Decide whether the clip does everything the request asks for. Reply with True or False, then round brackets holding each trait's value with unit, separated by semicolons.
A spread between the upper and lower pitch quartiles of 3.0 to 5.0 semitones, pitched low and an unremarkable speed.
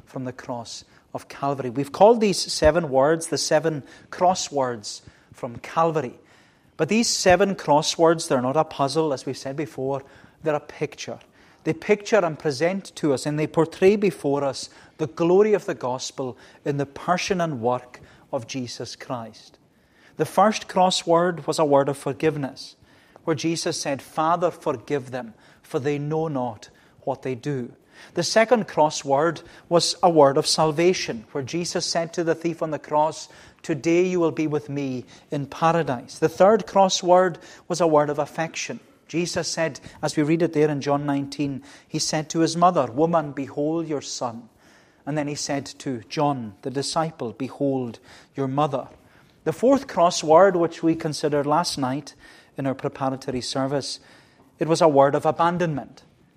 False (3.5 semitones; 155 Hz; 165 wpm)